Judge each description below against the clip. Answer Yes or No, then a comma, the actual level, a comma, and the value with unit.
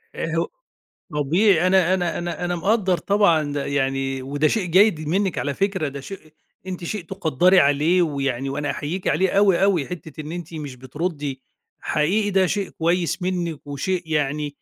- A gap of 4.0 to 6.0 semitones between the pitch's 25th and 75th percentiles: Yes, average, 4.5 semitones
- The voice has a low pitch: No, medium, 170 Hz